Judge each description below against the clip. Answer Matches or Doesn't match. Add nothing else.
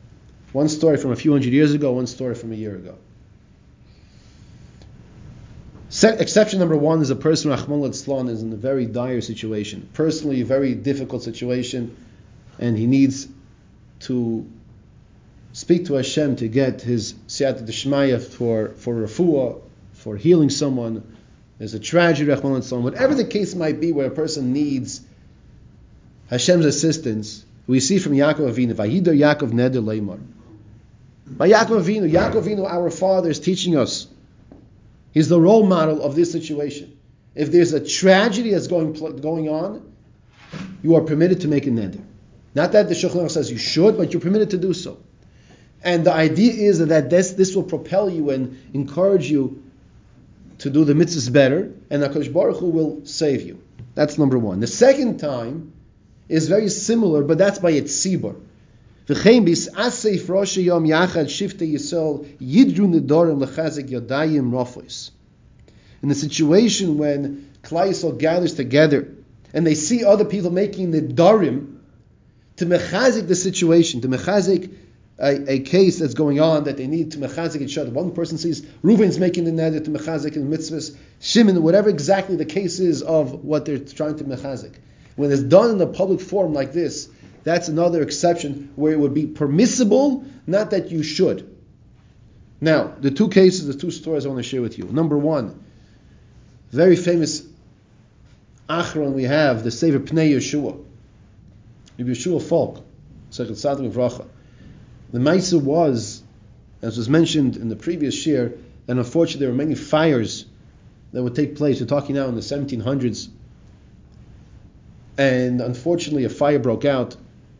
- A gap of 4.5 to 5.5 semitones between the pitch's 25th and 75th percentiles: Matches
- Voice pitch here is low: Doesn't match